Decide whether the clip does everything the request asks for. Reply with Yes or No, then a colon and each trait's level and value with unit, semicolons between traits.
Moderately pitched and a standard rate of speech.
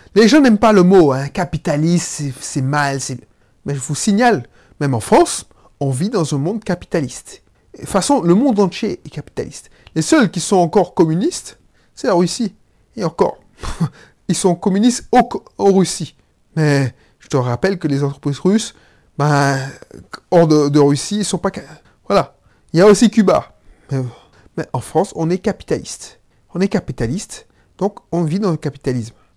Yes: medium, 170 Hz; average, 180 wpm